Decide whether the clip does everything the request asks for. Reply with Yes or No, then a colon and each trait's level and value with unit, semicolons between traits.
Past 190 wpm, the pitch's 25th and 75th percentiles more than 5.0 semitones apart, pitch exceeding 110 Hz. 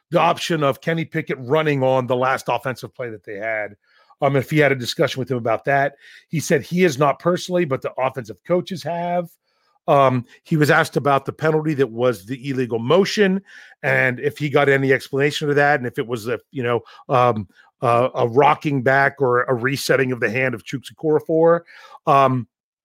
No: average, 200 wpm; average, 3.5 semitones; medium, 140 Hz